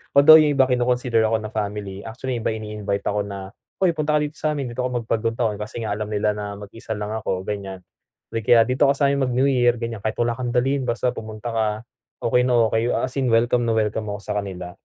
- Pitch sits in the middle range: No, low, 115 Hz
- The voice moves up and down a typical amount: Yes, average, 3.1 semitones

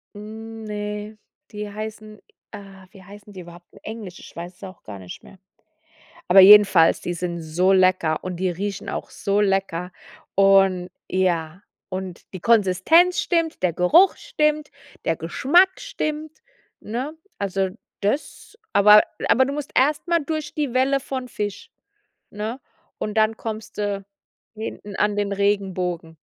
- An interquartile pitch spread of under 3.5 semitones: No, average, 3.8 semitones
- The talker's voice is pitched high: Yes, high, 205 Hz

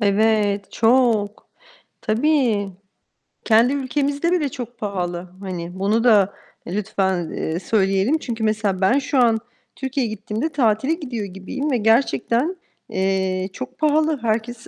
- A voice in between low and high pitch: No, high, 220 Hz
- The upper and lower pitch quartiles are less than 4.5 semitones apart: No, average, 4.9 semitones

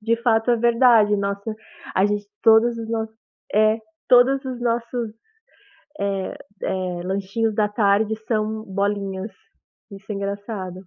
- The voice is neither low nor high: No, high, 215 Hz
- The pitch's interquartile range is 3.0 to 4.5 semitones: No, narrow, 2.5 semitones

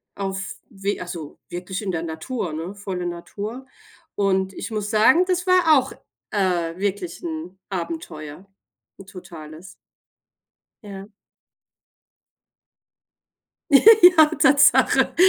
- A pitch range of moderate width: No, wide, 6.9 semitones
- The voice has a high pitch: Yes, high, 195 Hz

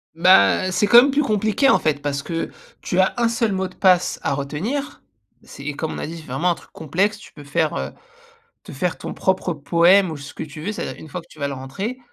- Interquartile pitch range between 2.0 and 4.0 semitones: No, average, 5.3 semitones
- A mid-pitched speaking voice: Yes, medium, 175 Hz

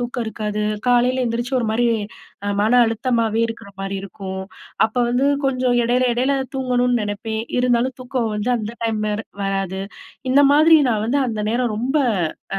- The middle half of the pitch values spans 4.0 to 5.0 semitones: No, average, 2.7 semitones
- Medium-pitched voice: No, high, 235 Hz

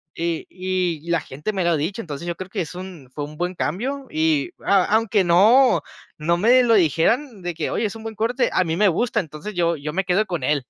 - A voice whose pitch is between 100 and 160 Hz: No, medium, 180 Hz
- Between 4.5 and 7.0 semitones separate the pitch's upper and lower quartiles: Yes, average, 4.9 semitones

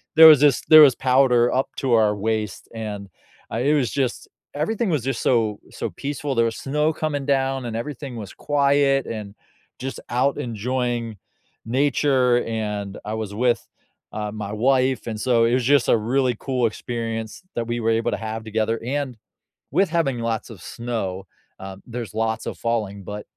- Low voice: Yes, low, 120 Hz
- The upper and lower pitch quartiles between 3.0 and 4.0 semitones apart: Yes, average, 3.4 semitones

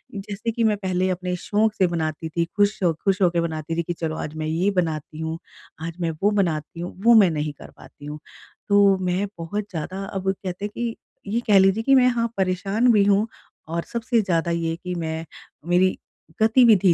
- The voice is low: No, medium, 185 Hz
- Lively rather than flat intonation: No, average, 3.7 semitones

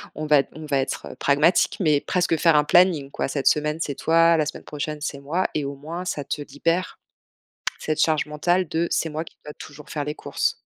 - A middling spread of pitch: No, narrow, 2.3 semitones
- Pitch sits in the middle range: Yes, medium, 150 Hz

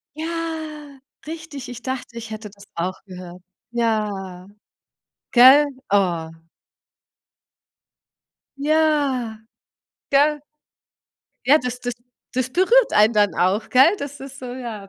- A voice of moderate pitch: No, very high, 250 Hz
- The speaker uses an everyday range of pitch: No, wide, 5.8 semitones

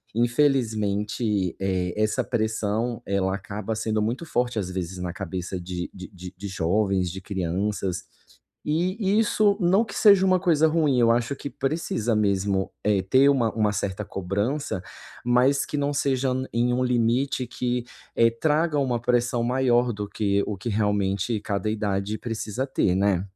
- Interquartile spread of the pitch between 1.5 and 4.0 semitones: No, average, 4.8 semitones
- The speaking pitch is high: No, low, 110 Hz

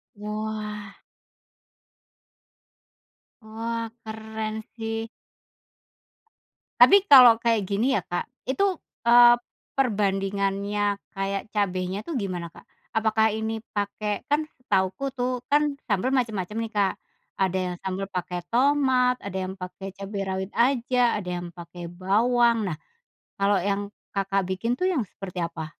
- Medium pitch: No, high, 210 Hz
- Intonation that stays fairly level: No, average, 3.5 semitones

